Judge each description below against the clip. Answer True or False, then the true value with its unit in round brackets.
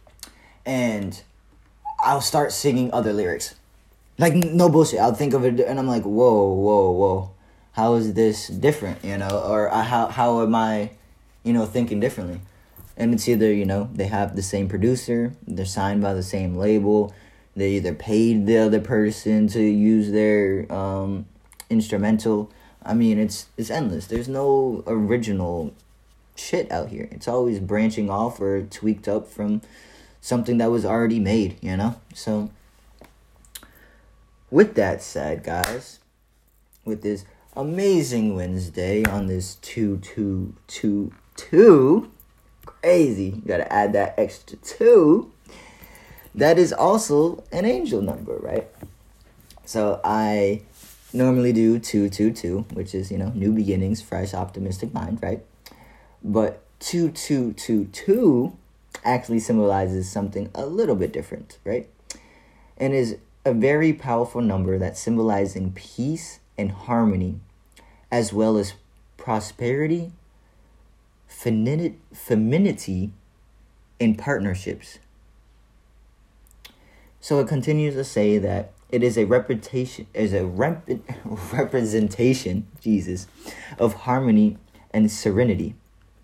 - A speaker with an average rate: False (130 wpm)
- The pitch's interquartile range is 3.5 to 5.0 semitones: False (3.1 semitones)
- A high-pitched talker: False (105 Hz)